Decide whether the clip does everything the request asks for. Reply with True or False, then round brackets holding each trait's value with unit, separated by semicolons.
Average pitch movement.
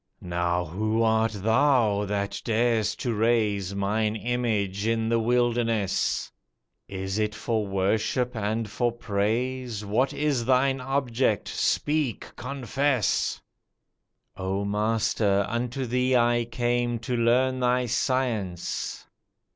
True (3.2 semitones)